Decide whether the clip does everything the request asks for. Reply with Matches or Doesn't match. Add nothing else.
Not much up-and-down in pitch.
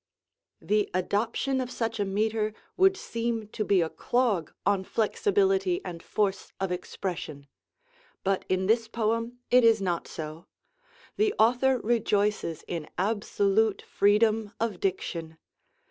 Doesn't match